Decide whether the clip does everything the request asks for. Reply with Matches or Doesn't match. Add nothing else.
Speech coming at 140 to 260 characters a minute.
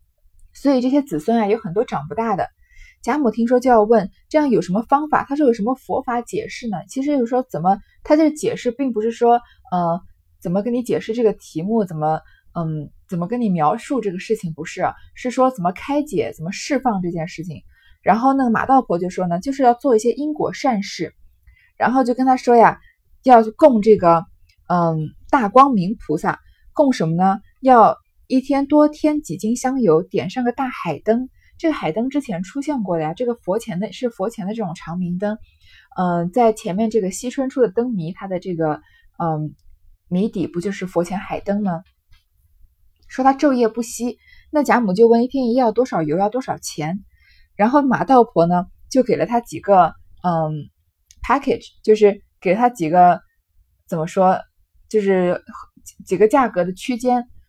Doesn't match